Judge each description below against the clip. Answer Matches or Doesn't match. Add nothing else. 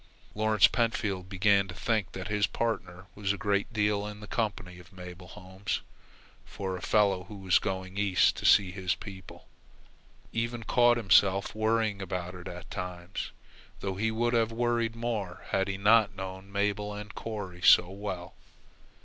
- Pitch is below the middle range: Matches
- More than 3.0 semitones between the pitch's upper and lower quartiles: Doesn't match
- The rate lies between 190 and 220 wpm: Doesn't match